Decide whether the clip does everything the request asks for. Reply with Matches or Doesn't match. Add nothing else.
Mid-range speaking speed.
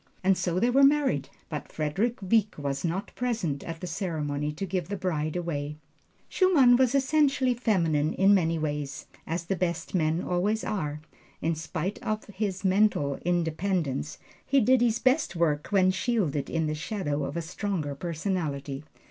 Matches